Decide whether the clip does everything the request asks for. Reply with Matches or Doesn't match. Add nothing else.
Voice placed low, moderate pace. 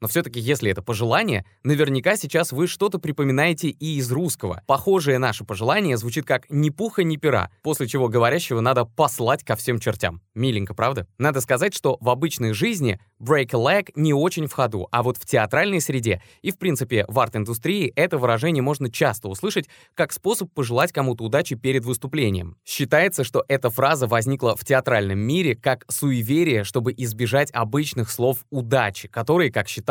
Doesn't match